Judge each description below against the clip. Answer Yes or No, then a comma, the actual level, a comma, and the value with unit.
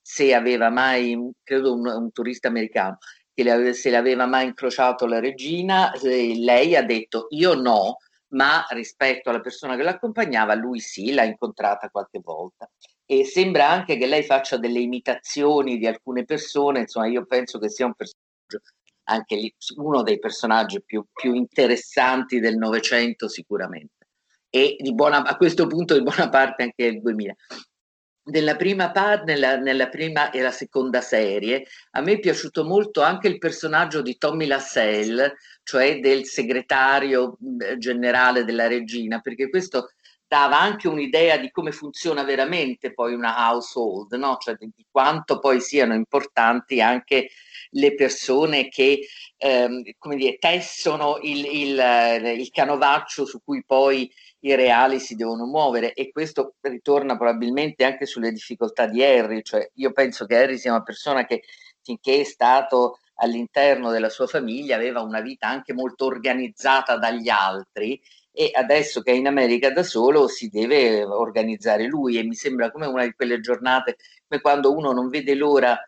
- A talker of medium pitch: No, low, 130 Hz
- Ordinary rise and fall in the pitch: Yes, average, 3.5 semitones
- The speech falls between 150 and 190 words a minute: Yes, average, 160 wpm